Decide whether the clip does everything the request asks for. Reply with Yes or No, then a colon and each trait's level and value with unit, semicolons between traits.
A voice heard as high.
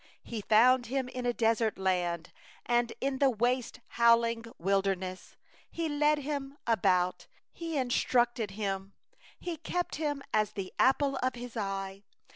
Yes: high, 235 Hz